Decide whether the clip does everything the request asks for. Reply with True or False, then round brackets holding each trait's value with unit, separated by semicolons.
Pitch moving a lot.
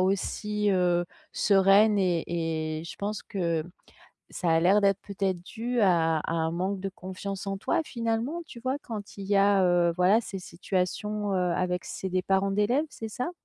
False (2.8 semitones)